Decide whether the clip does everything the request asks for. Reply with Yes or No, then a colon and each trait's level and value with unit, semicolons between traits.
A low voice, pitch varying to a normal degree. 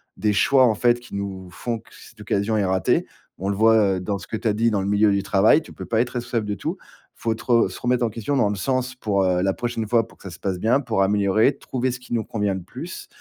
Yes: low, 110 Hz; average, 3.3 semitones